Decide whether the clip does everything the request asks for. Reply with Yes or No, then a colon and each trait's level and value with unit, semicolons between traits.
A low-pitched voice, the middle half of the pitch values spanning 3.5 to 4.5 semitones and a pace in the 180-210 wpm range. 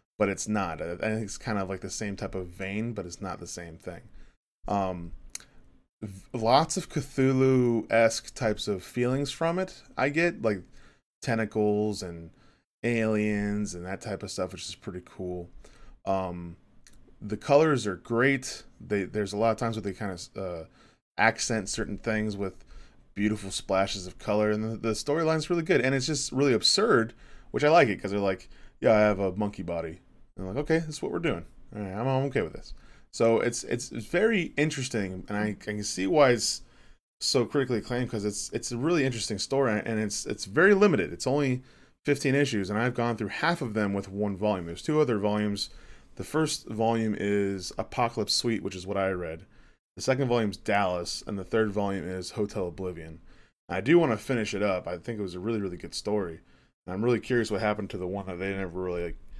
Yes: low, 105 Hz; average, 3.8 semitones; fast, 205 wpm